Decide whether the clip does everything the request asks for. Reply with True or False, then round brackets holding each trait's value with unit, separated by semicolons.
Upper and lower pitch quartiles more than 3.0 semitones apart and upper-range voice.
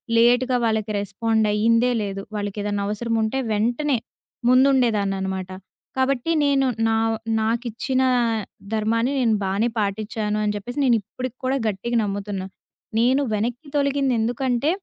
True (3.5 semitones; 230 Hz)